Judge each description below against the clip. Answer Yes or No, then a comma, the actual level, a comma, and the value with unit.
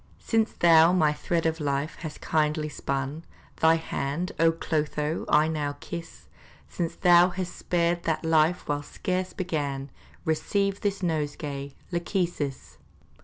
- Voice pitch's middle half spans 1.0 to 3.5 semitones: Yes, average, 2.8 semitones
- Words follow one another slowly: Yes, slow, 130 wpm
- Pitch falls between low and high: Yes, medium, 160 Hz